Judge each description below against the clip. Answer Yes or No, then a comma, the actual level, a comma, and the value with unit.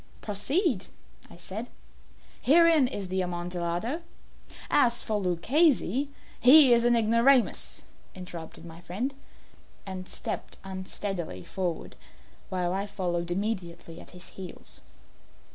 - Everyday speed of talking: No, slow, 115 wpm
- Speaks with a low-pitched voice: No, high, 195 Hz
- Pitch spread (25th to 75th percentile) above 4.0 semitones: Yes, wide, 5.5 semitones